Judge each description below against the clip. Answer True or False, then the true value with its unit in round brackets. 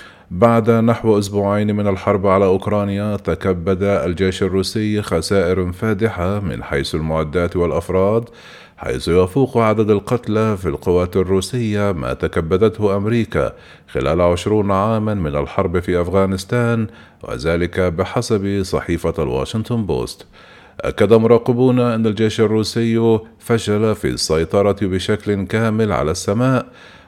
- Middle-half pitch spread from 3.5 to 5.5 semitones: False (3.0 semitones)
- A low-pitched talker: True (100 Hz)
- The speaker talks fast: False (110 wpm)